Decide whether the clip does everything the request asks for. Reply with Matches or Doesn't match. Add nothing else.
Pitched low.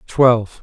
Matches